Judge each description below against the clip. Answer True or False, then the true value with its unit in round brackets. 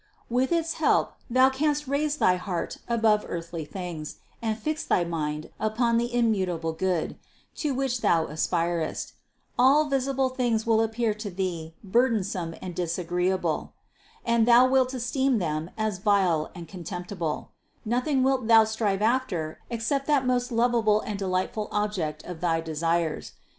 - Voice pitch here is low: False (215 Hz)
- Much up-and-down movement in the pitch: True (6.1 semitones)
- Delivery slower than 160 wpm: True (150 wpm)